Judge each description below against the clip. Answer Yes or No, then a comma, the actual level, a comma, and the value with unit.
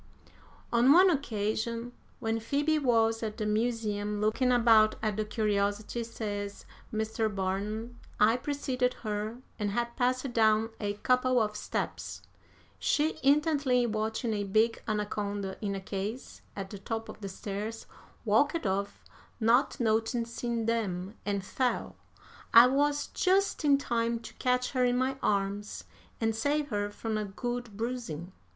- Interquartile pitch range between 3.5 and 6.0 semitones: No, average, 3.0 semitones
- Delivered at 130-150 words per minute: Yes, average, 145 wpm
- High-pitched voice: Yes, high, 225 Hz